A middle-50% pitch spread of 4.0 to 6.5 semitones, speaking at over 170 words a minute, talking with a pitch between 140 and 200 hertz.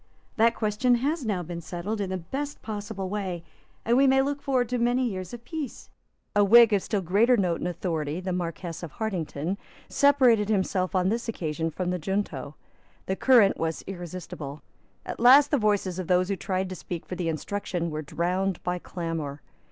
Yes: average, 4.9 semitones; average, 190 wpm; high, 190 Hz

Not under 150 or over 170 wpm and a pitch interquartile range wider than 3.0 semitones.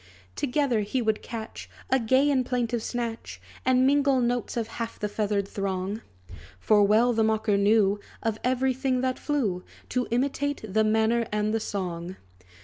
Yes: average, 160 wpm; average, 3.4 semitones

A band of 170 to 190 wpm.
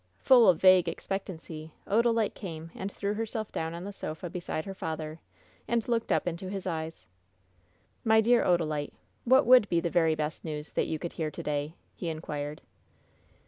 Yes: average, 180 wpm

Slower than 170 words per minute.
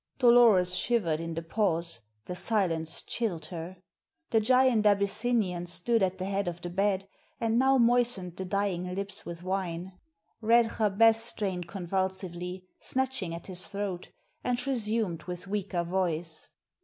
Yes: average, 145 wpm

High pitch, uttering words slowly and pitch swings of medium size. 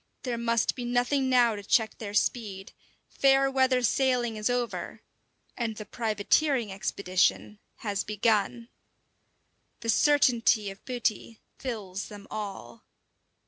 Yes: high, 230 Hz; slow, 120 wpm; average, 3.1 semitones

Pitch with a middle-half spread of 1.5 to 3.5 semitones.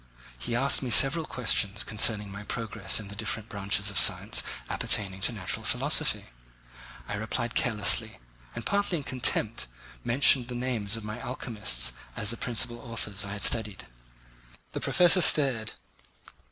Yes: average, 3.2 semitones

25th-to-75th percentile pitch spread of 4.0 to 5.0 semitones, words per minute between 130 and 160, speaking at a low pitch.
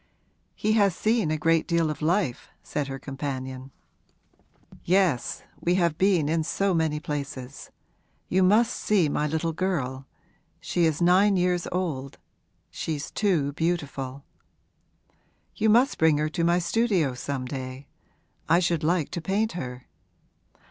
No: average, 4.4 semitones; average, 140 wpm; medium, 165 Hz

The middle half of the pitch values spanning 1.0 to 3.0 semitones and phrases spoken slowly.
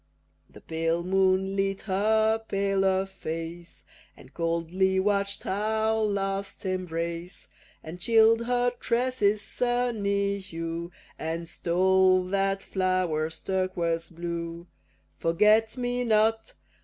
No: average, 3.9 semitones; slow, 100 wpm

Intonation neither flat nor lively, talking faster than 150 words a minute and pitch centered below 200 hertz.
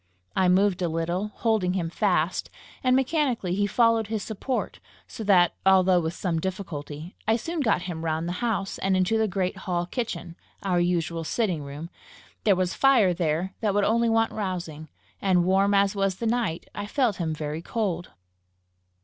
Yes: average, 4.0 semitones; average, 175 wpm; high, 190 Hz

